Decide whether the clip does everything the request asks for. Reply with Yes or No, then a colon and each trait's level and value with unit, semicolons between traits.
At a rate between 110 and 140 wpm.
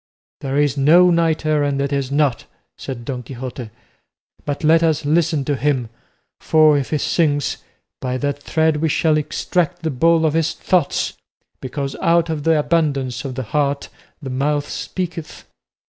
No: average, 160 wpm